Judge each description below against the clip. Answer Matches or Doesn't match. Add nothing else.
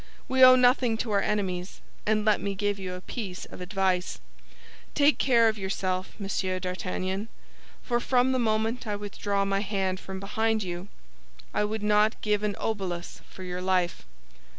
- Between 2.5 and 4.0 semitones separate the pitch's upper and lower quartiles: Matches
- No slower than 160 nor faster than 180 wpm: Matches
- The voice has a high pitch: Matches